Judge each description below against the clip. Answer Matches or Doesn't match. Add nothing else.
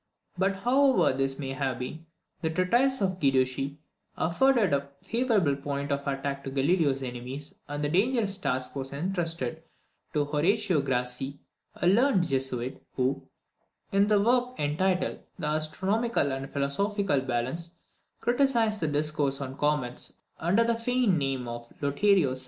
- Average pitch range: Doesn't match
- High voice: Doesn't match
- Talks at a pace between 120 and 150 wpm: Matches